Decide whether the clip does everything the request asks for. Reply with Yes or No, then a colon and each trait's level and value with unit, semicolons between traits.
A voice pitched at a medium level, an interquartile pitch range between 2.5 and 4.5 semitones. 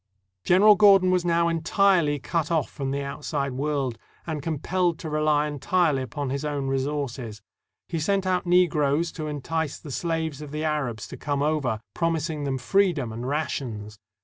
Yes: medium, 150 Hz; average, 3.4 semitones